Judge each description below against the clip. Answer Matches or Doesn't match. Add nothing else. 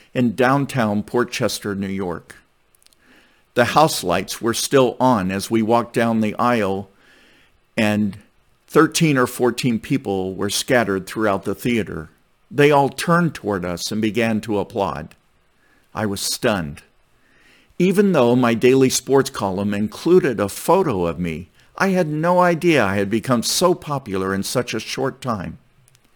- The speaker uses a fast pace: Doesn't match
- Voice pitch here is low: Matches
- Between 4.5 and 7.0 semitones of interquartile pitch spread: Matches